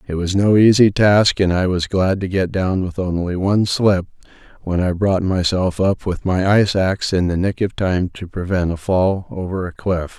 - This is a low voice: Yes, very low, 95 Hz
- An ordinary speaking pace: No, fast, 220 wpm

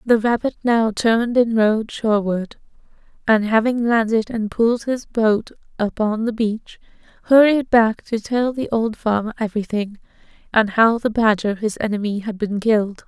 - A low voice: No, high, 220 Hz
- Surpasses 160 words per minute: No, average, 155 wpm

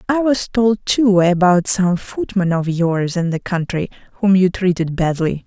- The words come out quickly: No, average, 175 wpm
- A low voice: No, high, 190 Hz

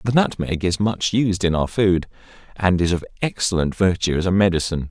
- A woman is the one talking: No, male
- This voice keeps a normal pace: Yes, average, 195 wpm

